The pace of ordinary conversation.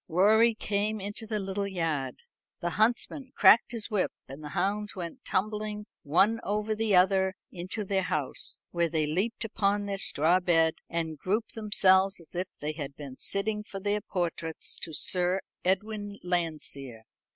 Yes: average, 160 wpm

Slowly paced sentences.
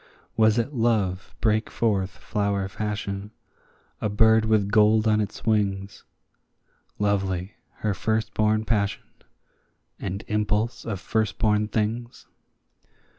Yes: slow, 105 wpm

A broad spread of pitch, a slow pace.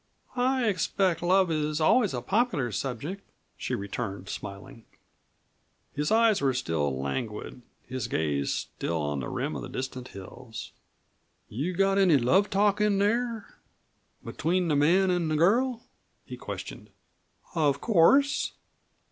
Yes: wide, 8.4 semitones; slow, 130 wpm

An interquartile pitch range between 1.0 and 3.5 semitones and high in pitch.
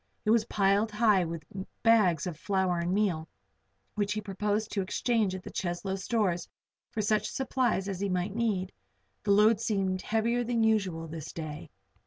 Yes: average, 3.1 semitones; high, 200 Hz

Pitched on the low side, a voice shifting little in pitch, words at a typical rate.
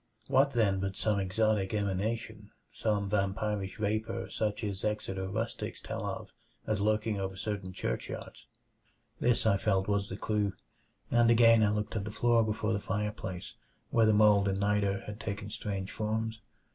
Yes: low, 105 Hz; narrow, 1.8 semitones; average, 160 wpm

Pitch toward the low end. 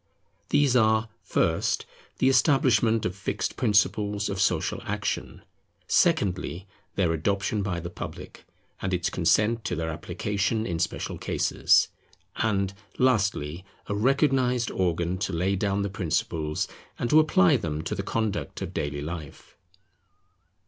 Yes: low, 100 Hz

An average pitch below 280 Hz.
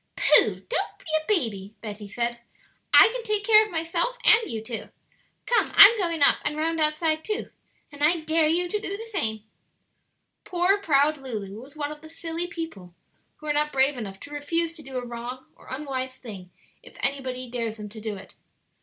No: very high, 300 Hz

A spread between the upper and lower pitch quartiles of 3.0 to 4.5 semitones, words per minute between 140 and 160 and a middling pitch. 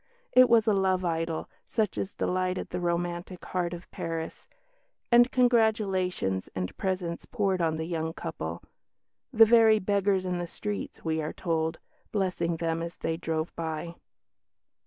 Yes: average, 3.5 semitones; average, 150 wpm; medium, 180 Hz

